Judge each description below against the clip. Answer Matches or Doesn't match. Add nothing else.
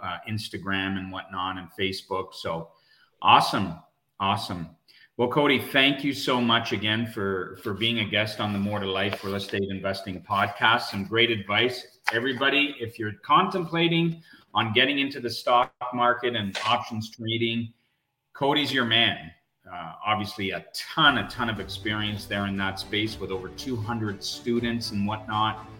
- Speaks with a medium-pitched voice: Doesn't match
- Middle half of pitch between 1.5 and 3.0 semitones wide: Doesn't match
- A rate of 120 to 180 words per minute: Matches